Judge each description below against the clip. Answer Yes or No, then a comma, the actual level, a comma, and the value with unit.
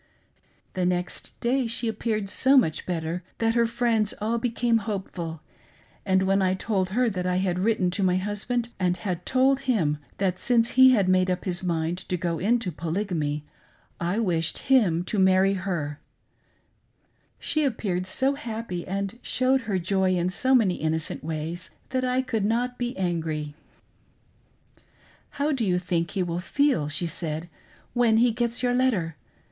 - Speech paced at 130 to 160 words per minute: No, average, 170 wpm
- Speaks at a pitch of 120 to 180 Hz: No, high, 190 Hz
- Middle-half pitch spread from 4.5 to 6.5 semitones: Yes, average, 5.0 semitones